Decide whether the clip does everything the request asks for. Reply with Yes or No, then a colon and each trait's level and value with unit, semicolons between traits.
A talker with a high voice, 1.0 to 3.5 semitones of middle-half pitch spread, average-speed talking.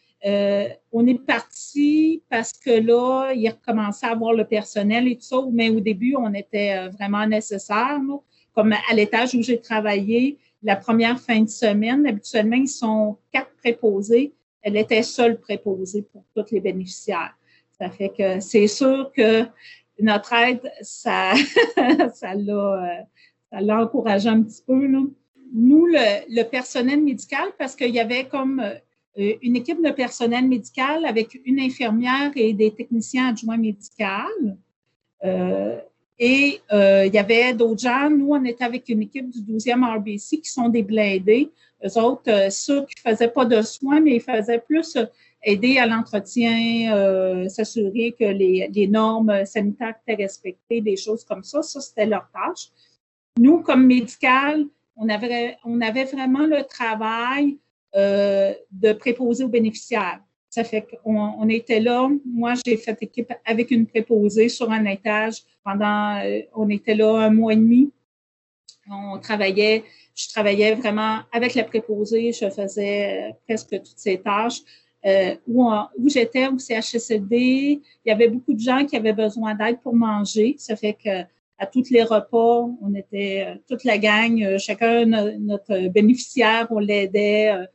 Yes: high, 225 Hz; average, 3.0 semitones; average, 160 wpm